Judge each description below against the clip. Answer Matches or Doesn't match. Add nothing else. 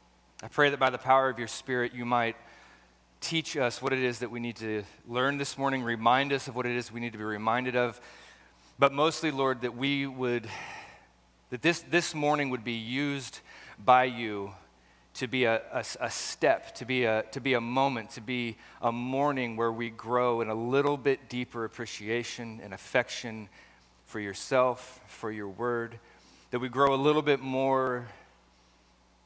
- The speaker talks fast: Doesn't match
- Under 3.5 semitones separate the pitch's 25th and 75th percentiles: Matches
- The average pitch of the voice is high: Doesn't match